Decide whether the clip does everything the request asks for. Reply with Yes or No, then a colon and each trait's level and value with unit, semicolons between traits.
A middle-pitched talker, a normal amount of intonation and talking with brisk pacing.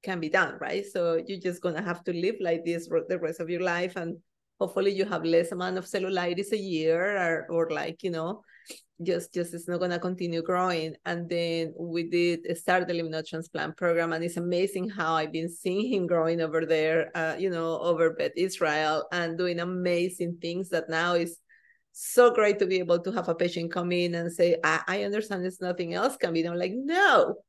No: medium, 175 Hz; narrow, 1.9 semitones; fast, 220 wpm